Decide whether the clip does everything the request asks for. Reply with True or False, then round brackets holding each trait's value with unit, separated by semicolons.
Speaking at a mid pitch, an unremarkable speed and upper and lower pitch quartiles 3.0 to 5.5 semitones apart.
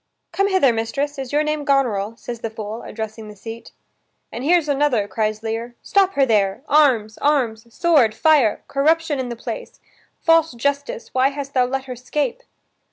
False (260 Hz; 170 wpm; 4.7 semitones)